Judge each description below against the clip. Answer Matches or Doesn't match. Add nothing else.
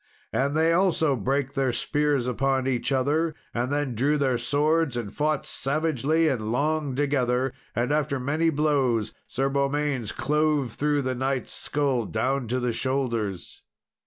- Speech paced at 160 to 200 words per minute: Doesn't match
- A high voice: Doesn't match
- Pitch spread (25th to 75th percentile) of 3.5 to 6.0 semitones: Doesn't match